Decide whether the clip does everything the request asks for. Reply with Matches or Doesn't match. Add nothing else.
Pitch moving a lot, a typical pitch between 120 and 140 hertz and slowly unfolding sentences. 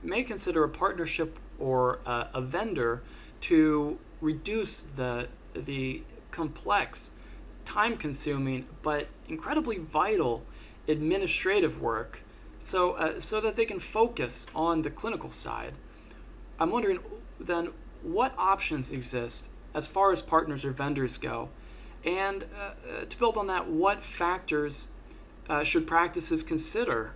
Doesn't match